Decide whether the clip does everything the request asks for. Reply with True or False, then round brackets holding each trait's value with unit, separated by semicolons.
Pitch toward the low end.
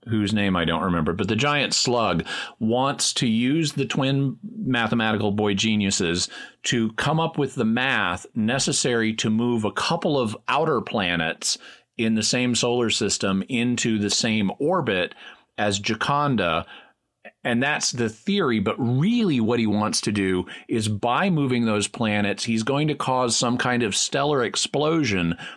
True (115 Hz)